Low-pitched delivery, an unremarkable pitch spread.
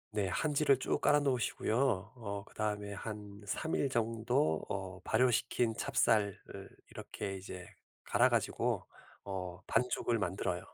Yes: low, 105 Hz; average, 4.0 semitones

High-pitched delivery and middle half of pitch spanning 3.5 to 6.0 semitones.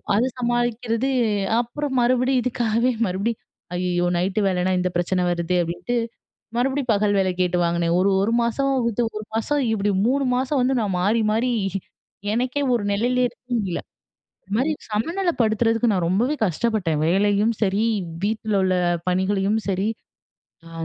Yes: high, 220 Hz; average, 4.5 semitones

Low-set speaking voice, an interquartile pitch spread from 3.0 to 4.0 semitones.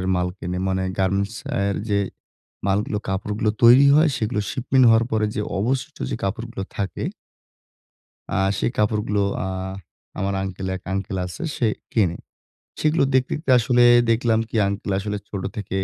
Yes: low, 105 Hz; average, 3.3 semitones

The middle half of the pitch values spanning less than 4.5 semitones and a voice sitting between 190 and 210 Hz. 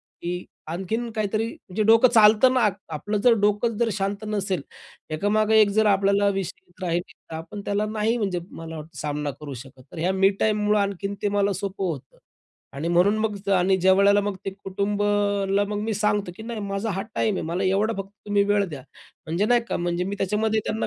Yes: narrow, 2.5 semitones; high, 200 Hz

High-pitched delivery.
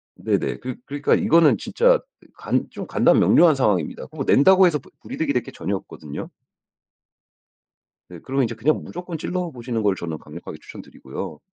No: low, 135 Hz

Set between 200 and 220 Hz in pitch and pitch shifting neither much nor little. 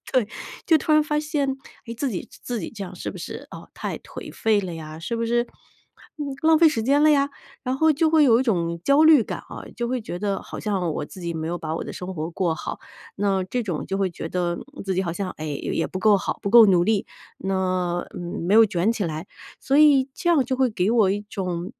No: high, 205 Hz; wide, 6.5 semitones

